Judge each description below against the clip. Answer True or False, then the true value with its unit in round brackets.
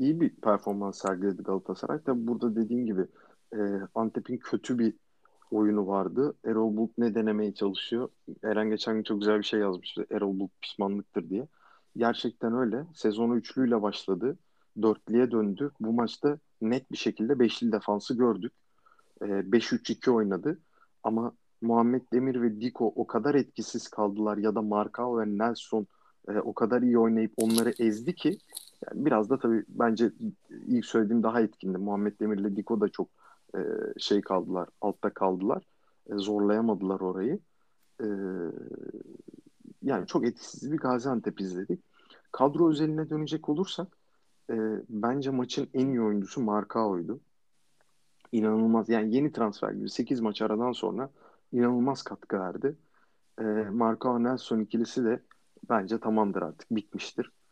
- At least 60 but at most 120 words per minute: False (135 wpm)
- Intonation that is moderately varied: True (3.0 semitones)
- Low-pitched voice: True (115 Hz)